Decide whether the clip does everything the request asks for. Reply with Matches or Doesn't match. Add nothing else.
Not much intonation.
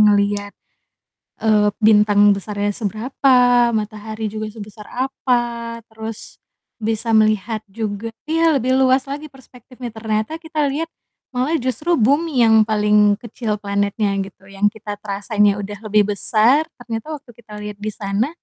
Doesn't match